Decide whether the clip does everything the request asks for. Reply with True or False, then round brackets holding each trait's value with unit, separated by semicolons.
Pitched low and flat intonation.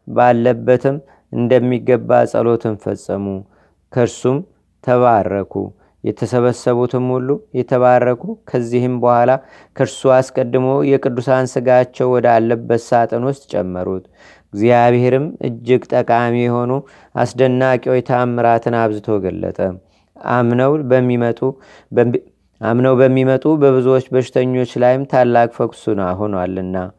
True (125 Hz; 1.9 semitones)